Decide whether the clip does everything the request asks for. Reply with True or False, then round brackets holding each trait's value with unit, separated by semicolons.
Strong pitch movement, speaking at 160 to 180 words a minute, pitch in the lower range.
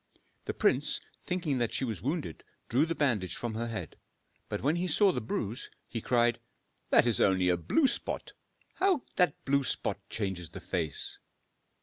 True (7.7 semitones; 175 wpm; 120 Hz)